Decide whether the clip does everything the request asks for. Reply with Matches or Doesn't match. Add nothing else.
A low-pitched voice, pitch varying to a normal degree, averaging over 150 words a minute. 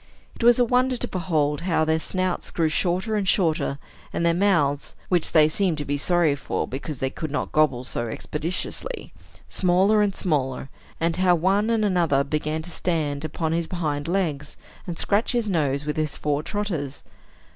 Doesn't match